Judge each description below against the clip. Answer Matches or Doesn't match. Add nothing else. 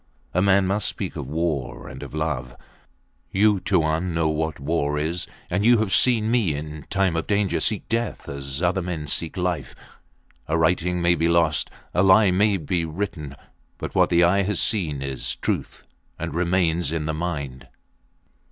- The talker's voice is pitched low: Matches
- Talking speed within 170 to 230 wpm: Matches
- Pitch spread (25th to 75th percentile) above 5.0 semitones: Doesn't match